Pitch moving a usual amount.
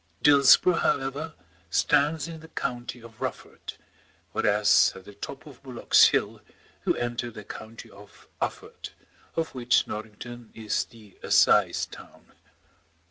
Yes: average, 4.3 semitones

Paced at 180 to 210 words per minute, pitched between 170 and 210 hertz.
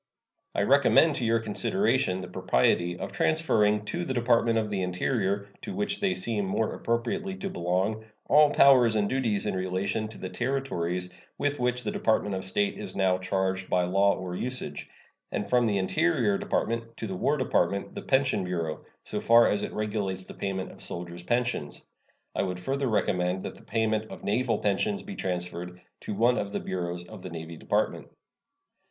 No: average, 185 wpm; low, 105 Hz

